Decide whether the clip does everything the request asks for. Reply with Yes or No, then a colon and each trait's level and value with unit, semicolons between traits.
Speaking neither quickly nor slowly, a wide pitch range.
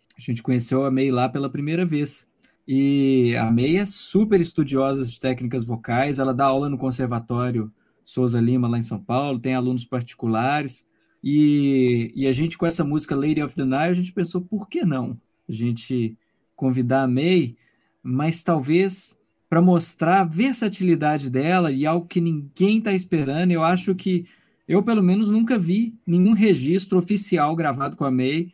Yes: average, 170 wpm; wide, 5.8 semitones